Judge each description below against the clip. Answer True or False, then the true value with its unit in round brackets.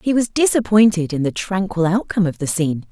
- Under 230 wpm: True (205 wpm)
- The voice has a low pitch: False (190 Hz)